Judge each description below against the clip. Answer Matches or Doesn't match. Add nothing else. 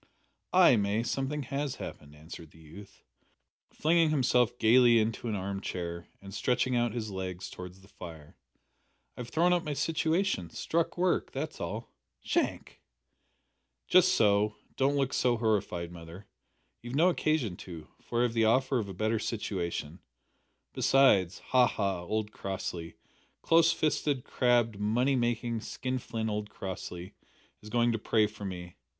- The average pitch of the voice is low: Matches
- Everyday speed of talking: Matches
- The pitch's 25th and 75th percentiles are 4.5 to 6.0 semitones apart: Matches